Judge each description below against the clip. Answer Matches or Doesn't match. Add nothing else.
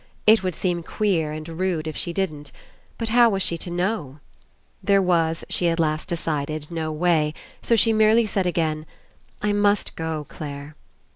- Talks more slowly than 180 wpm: Doesn't match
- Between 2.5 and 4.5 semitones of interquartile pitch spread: Matches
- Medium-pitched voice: Matches